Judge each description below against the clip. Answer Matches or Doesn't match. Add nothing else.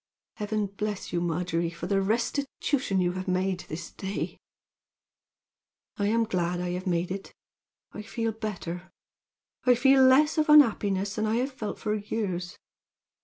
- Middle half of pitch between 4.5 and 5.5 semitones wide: Doesn't match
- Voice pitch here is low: Doesn't match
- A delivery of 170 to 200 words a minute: Doesn't match